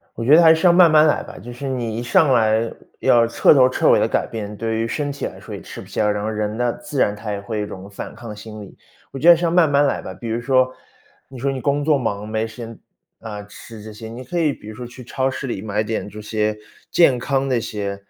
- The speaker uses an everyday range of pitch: Yes, average, 4.2 semitones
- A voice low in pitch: Yes, low, 115 Hz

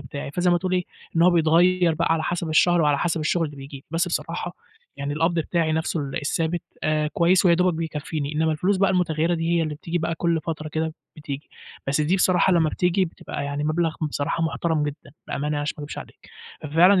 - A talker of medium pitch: Yes, medium, 165 Hz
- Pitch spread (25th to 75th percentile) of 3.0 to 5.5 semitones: No, narrow, 2.4 semitones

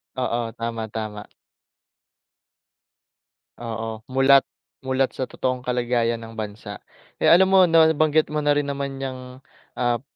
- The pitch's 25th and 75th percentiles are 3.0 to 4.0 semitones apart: Yes, average, 3.4 semitones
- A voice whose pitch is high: No, low, 130 Hz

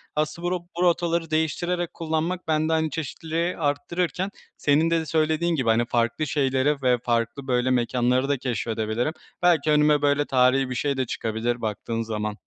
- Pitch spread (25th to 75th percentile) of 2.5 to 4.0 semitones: No, average, 4.7 semitones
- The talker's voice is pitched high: No, medium, 145 Hz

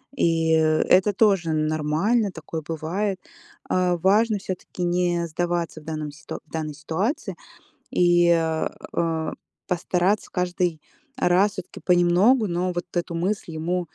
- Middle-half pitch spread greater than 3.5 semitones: No, narrow, 2.4 semitones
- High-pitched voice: No, medium, 175 Hz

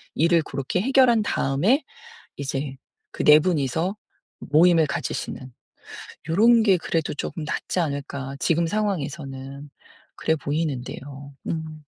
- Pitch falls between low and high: Yes, medium, 155 Hz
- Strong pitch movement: No, average, 4.2 semitones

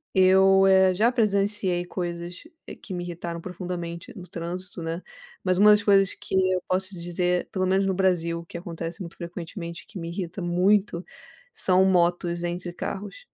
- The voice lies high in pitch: No, medium, 180 Hz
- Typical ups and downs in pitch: No, narrow, 1.9 semitones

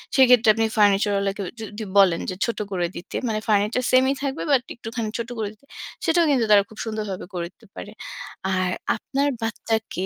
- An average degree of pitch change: Yes, average, 3.3 semitones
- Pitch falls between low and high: No, high, 220 Hz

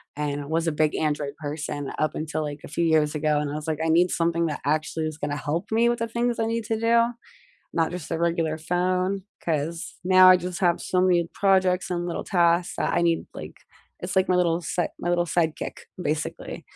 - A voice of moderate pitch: Yes, medium, 170 Hz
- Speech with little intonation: No, average, 3.0 semitones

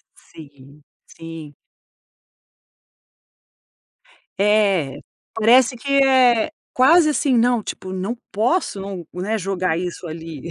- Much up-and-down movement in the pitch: Yes, wide, 6.7 semitones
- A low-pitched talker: No, high, 195 Hz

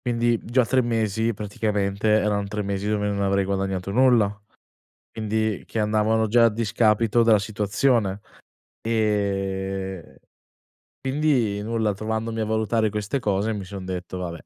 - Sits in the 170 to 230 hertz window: No, low, 105 Hz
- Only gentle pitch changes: Yes, narrow, 2.3 semitones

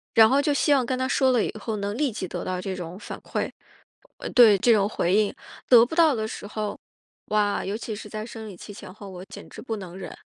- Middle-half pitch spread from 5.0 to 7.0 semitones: No, average, 3.5 semitones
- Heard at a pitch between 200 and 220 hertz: Yes, high, 215 Hz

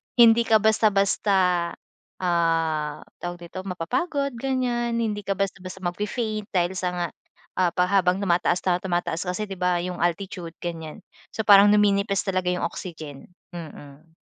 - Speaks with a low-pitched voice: No, medium, 185 Hz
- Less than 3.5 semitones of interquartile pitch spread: Yes, average, 3.1 semitones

